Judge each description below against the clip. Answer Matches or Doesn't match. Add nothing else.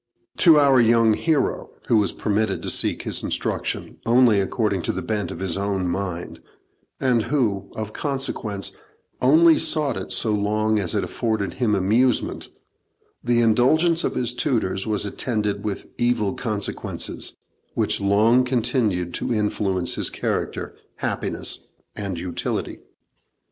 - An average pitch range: Matches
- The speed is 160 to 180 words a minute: Doesn't match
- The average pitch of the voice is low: Matches